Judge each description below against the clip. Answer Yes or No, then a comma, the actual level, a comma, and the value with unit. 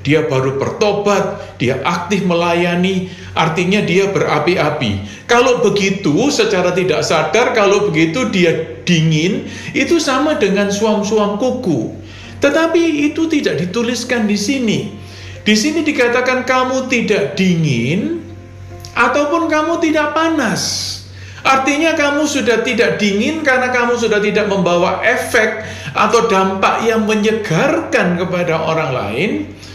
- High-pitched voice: Yes, high, 205 Hz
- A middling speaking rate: Yes, average, 115 wpm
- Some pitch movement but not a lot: No, wide, 7.3 semitones